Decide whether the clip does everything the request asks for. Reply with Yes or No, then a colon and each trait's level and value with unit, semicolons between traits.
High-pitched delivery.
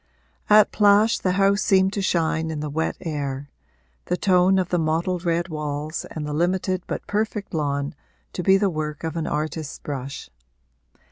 No: medium, 165 Hz